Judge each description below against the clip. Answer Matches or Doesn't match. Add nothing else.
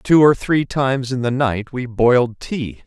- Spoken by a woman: Doesn't match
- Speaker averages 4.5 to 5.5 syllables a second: Doesn't match